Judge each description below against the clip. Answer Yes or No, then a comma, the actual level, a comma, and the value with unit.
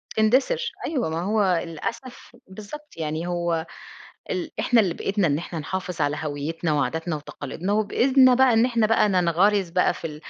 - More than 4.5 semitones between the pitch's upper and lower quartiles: Yes, wide, 5.6 semitones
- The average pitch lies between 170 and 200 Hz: Yes, medium, 185 Hz